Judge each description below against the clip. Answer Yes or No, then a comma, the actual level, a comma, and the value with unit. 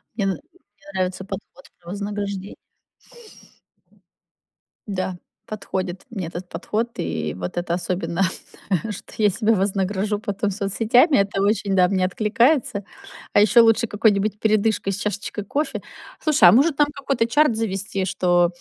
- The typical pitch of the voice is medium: No, high, 200 Hz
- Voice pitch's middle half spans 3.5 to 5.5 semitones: No, average, 2.9 semitones